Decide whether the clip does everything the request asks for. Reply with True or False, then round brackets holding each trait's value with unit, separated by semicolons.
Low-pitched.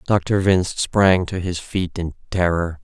True (90 Hz)